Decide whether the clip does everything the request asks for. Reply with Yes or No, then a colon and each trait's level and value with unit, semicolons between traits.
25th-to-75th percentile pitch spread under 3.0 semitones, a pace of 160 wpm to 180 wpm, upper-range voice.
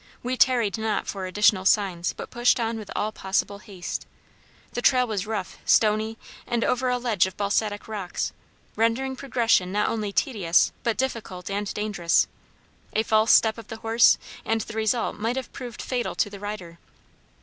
Yes: narrow, 2.6 semitones; average, 170 wpm; high, 215 Hz